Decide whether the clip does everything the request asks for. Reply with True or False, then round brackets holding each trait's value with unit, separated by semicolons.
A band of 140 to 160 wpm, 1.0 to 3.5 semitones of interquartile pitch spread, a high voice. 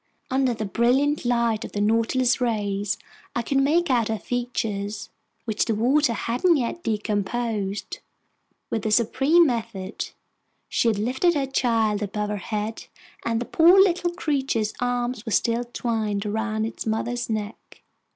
True (150 wpm; 3.1 semitones; 230 Hz)